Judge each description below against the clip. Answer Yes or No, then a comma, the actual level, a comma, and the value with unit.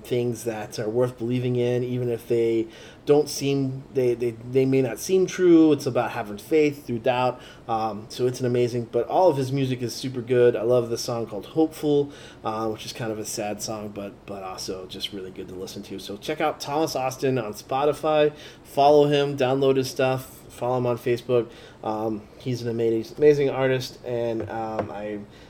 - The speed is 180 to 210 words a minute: Yes, average, 200 wpm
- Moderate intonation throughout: Yes, average, 3.2 semitones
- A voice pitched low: Yes, low, 125 Hz